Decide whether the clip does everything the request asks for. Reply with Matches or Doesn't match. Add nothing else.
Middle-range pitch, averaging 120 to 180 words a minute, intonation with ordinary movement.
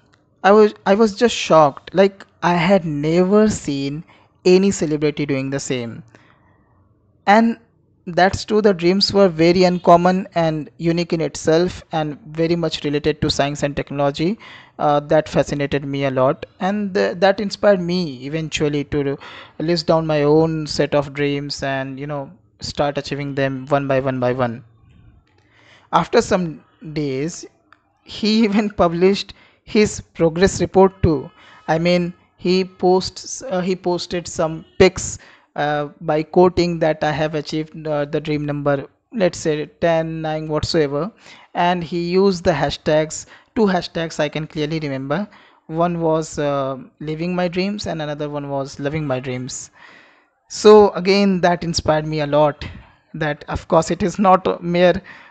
Matches